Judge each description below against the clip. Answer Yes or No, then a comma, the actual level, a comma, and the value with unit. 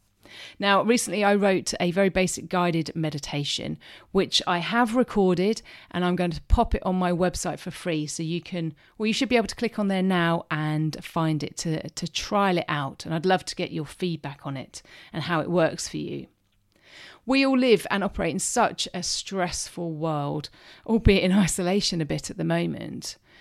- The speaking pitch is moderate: Yes, medium, 180 Hz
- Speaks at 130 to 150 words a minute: No, average, 200 wpm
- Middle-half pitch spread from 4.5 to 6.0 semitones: No, average, 3.8 semitones